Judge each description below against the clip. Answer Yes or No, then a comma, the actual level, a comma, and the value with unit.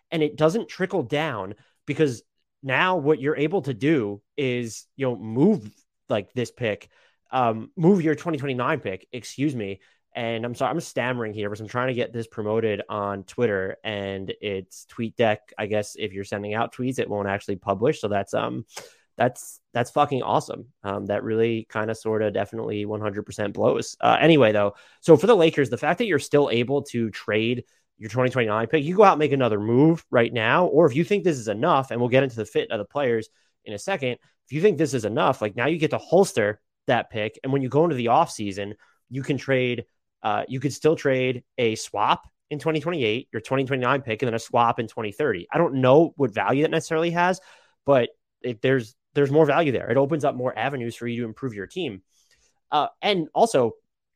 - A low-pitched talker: Yes, low, 125 Hz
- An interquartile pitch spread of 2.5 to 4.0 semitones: No, average, 5.3 semitones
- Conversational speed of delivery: No, fast, 215 wpm